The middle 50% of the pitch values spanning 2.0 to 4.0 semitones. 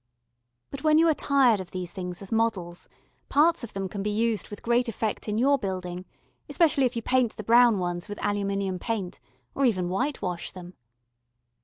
No: average, 4.9 semitones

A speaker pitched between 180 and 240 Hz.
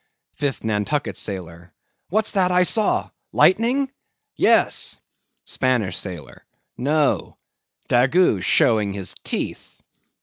No: low, 130 Hz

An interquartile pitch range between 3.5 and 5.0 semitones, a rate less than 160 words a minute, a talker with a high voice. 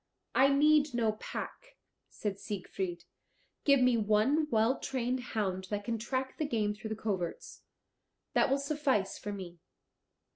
Yes: average, 4.7 semitones; average, 145 wpm; high, 225 Hz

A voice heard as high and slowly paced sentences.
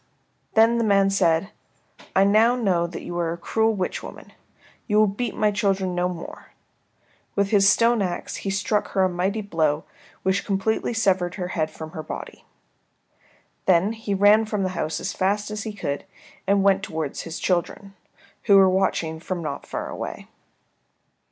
No: high, 195 Hz; average, 175 wpm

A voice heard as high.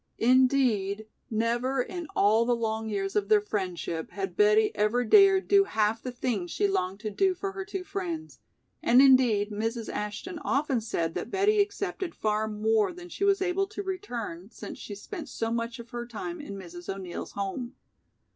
Yes: high, 240 Hz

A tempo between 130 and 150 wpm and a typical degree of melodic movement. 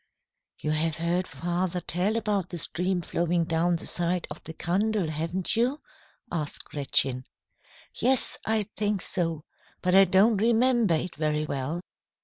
Yes: average, 145 wpm; average, 3.8 semitones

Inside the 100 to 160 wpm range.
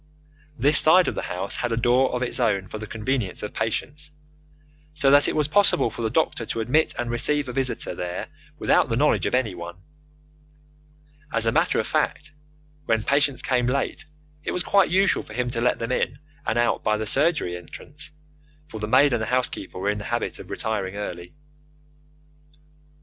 No: average, 195 wpm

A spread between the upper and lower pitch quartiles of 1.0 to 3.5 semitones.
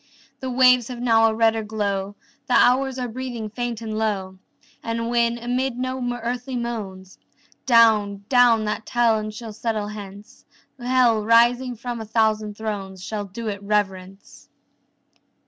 Yes: narrow, 2.6 semitones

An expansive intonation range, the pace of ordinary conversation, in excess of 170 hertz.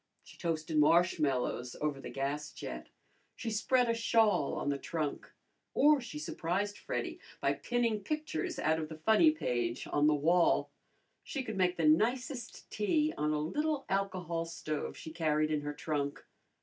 No: wide, 6.7 semitones; average, 160 wpm; medium, 165 Hz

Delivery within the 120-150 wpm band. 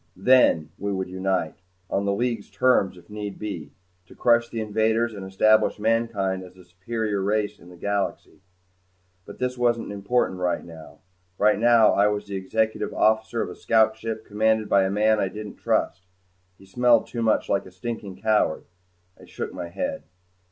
No: average, 180 wpm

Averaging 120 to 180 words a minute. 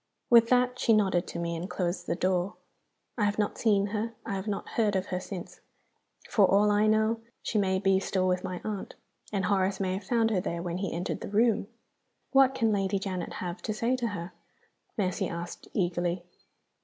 No: fast, 205 wpm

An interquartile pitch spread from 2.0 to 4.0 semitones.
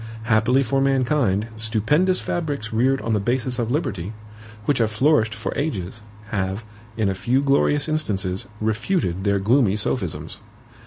No: average, 4.6 semitones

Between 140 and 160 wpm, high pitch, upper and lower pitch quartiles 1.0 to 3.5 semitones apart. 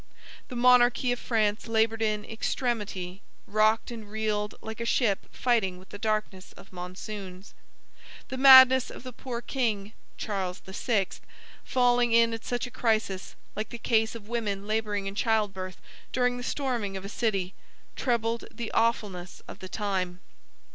Yes: average, 155 wpm; high, 220 Hz; average, 3.2 semitones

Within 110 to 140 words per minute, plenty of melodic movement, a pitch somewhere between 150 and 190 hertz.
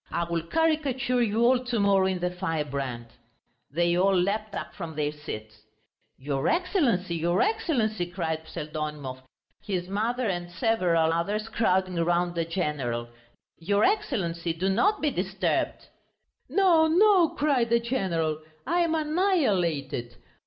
Yes: slow, 135 wpm; wide, 7.0 semitones; medium, 185 Hz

